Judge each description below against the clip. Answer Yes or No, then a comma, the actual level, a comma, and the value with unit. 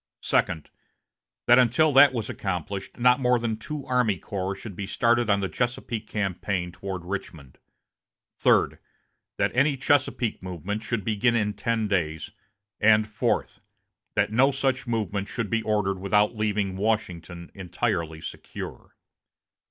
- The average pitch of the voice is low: Yes, low, 105 Hz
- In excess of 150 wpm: No, slow, 135 wpm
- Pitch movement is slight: No, average, 3.8 semitones